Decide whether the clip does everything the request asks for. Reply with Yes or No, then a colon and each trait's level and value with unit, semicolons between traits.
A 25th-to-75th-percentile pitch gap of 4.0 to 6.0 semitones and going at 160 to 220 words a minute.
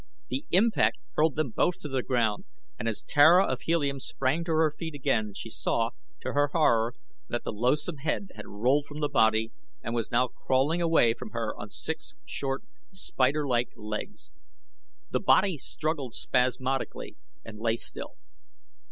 Yes: average, 5.0 semitones; average, 165 wpm